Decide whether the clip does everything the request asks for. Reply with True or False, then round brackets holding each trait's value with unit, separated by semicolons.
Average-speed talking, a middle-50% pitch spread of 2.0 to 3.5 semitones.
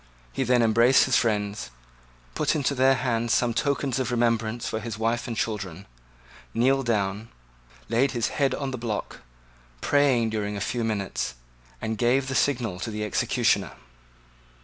True (155 wpm; 3.0 semitones)